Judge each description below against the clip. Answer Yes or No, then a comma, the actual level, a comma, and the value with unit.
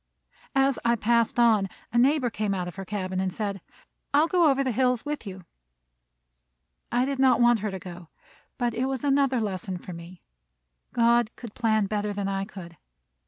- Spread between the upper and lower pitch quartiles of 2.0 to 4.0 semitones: No, average, 4.6 semitones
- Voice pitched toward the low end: No, high, 225 Hz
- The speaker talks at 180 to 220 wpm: Yes, average, 190 wpm